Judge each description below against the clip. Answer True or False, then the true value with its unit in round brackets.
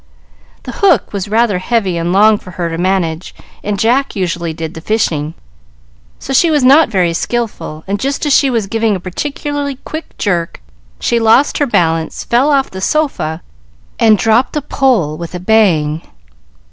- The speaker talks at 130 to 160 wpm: False (170 wpm)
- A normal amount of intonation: False (7.0 semitones)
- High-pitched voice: True (210 Hz)